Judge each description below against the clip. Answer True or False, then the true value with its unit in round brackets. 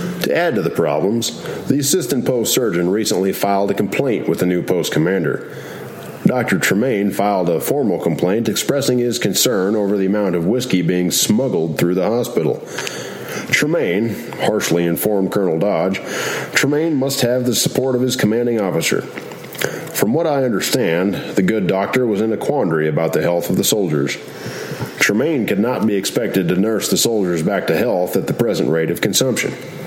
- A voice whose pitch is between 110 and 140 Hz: False (100 Hz)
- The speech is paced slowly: False (175 wpm)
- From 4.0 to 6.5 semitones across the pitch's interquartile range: True (5.5 semitones)